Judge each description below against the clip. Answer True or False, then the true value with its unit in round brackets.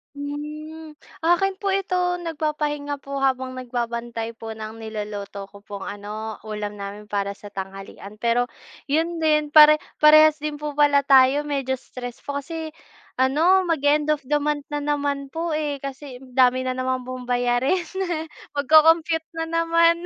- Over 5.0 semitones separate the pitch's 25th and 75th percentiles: False (4.0 semitones)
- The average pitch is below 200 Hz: False (285 Hz)